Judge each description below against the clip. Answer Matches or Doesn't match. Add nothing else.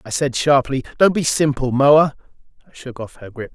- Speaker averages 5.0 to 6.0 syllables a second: Matches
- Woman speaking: Doesn't match